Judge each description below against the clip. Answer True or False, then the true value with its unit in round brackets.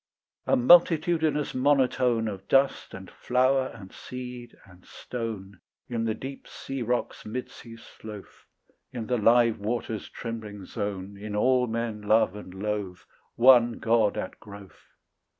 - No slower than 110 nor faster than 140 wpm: True (135 wpm)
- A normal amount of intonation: True (3.4 semitones)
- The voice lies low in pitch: True (115 Hz)